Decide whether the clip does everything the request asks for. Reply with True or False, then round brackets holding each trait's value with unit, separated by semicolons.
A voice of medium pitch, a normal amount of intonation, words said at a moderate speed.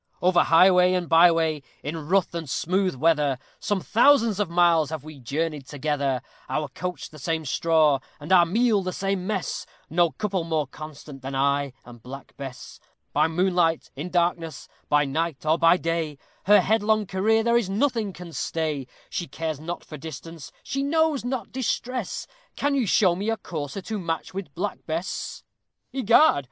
True (170 Hz; 4.4 semitones; 170 wpm)